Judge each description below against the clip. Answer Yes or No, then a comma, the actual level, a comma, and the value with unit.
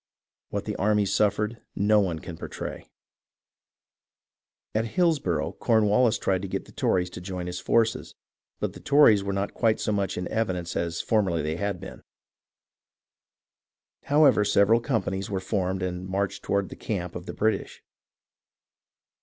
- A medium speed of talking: Yes, average, 150 wpm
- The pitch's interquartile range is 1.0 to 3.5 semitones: Yes, average, 3.0 semitones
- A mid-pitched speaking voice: No, low, 100 Hz